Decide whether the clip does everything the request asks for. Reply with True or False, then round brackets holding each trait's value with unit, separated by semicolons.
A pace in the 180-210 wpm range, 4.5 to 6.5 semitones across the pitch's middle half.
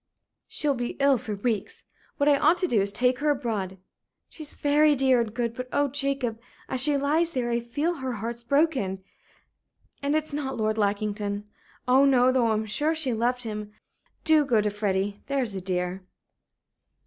True (185 wpm; 4.9 semitones)